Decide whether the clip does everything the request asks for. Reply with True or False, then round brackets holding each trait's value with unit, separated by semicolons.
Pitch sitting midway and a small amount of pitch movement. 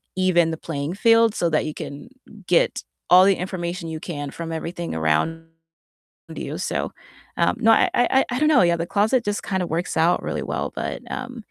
False (175 Hz; 4.6 semitones)